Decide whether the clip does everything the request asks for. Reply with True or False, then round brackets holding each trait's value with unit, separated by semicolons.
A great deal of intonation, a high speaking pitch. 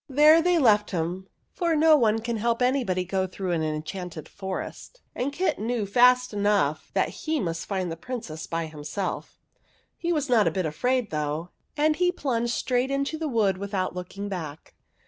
True (6.5 semitones; 210 Hz)